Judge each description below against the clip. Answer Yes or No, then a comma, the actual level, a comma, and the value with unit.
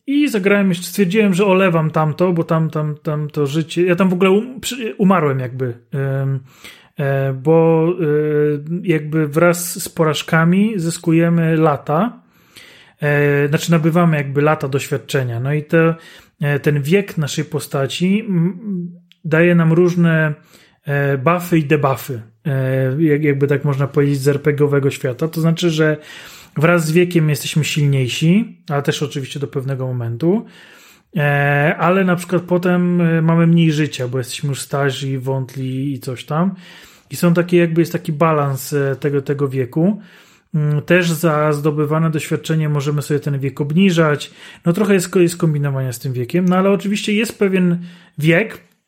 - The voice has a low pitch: No, medium, 160 Hz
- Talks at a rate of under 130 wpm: No, average, 140 wpm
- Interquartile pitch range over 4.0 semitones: No, average, 3.4 semitones